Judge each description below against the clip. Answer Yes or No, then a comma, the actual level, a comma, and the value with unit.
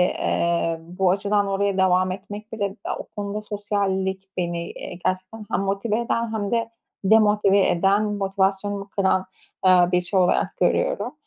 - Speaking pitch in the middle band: No, high, 195 Hz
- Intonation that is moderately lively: No, narrow, 1.9 semitones